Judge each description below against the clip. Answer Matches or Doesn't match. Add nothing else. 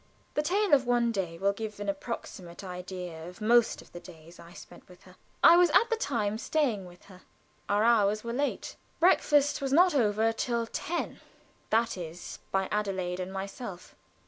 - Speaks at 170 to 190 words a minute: Matches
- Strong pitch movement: Doesn't match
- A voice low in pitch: Doesn't match